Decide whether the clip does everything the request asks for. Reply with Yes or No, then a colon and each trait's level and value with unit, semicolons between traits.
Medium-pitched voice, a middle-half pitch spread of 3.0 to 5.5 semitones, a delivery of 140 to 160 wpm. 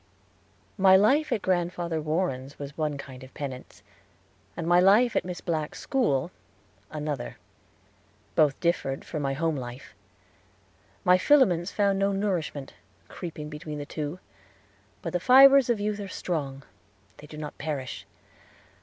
Yes: medium, 165 Hz; average, 4.9 semitones; average, 145 wpm